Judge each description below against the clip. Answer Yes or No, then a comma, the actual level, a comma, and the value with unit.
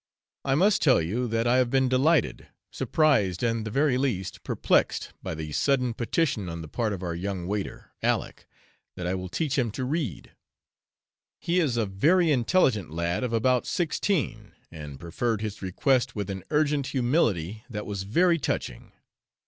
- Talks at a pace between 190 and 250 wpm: No, average, 170 wpm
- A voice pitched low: Yes, low, 115 Hz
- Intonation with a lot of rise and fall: Yes, wide, 6.4 semitones